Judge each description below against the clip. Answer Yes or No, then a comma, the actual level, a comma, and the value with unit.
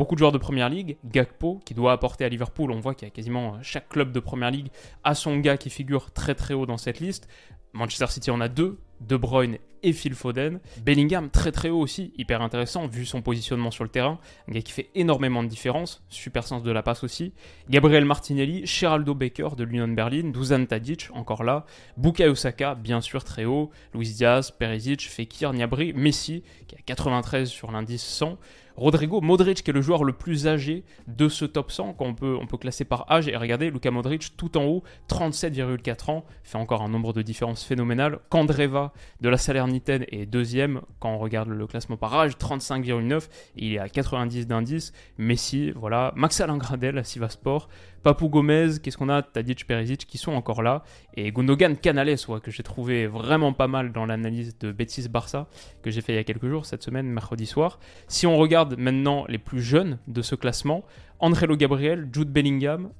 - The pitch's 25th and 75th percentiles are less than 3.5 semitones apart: No, average, 4.1 semitones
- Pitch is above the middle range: No, low, 130 Hz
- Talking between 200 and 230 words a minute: Yes, average, 205 wpm